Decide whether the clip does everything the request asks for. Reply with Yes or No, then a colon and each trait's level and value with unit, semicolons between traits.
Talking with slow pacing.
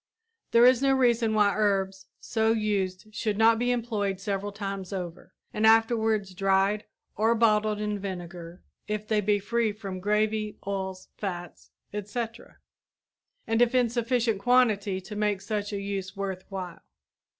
No: average, 150 wpm